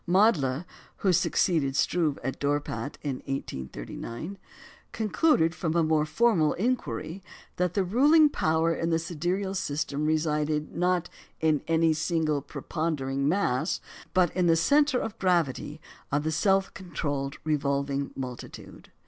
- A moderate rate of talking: No, slow, 130 wpm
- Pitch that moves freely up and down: No, average, 4.0 semitones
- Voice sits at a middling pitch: Yes, medium, 160 Hz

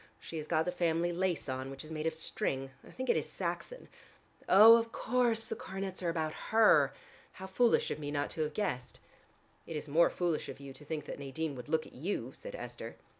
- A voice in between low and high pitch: Yes, medium, 160 Hz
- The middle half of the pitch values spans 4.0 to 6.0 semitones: Yes, average, 4.5 semitones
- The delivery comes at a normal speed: No, fast, 225 wpm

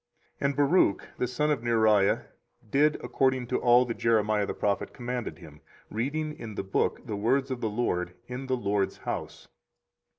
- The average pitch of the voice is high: No, low, 120 Hz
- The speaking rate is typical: Yes, average, 175 wpm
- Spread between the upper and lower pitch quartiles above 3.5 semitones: Yes, average, 4.1 semitones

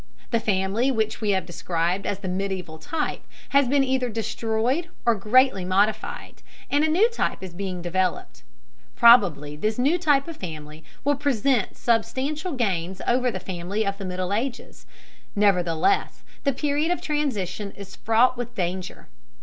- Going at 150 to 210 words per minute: Yes, average, 155 wpm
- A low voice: No, high, 220 Hz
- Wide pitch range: Yes, wide, 6.0 semitones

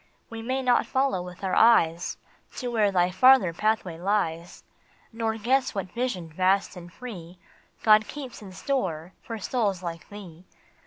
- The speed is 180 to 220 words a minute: No, average, 155 wpm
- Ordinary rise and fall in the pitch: Yes, average, 4.8 semitones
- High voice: Yes, high, 200 Hz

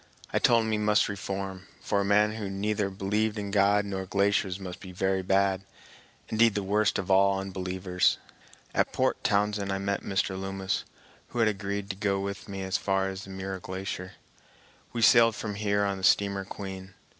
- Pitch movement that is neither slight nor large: No, narrow, 1.2 semitones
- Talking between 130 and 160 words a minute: No, average, 190 wpm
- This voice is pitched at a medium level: No, low, 100 Hz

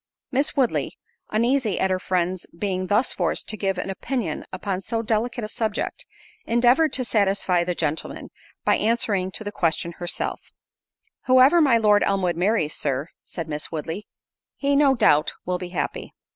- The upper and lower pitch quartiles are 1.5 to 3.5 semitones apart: No, average, 4.8 semitones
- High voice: Yes, high, 205 Hz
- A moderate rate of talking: Yes, average, 160 wpm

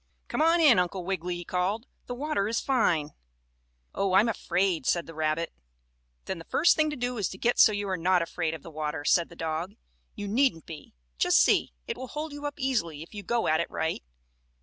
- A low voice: No, high, 190 Hz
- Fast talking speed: Yes, fast, 220 wpm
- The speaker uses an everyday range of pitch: No, wide, 6.7 semitones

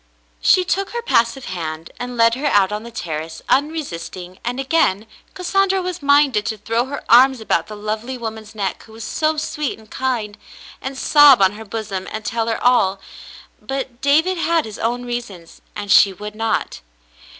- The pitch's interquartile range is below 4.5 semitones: No, average, 4.9 semitones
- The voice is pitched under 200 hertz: No, high, 230 Hz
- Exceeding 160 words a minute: Yes, average, 185 wpm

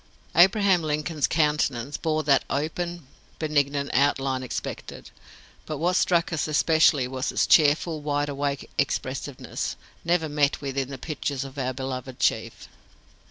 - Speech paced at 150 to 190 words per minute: No, slow, 135 wpm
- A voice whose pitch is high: No, medium, 145 Hz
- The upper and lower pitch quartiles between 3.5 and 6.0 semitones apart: No, average, 2.7 semitones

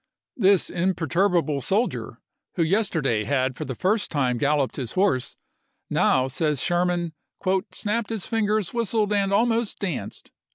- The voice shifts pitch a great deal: Yes, wide, 6.3 semitones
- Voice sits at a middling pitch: Yes, medium, 180 Hz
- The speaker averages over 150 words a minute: No, average, 140 wpm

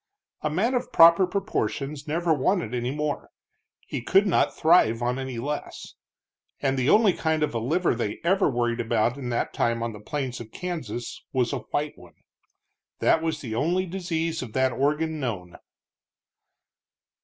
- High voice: No, medium, 145 Hz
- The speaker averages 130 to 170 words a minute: Yes, average, 165 wpm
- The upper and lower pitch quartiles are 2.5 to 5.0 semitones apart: No, wide, 5.6 semitones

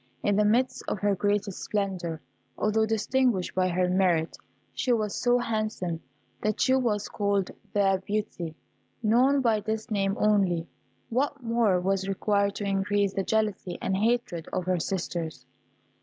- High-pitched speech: Yes, high, 205 Hz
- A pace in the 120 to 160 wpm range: Yes, average, 150 wpm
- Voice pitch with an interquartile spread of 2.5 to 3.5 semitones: Yes, average, 2.8 semitones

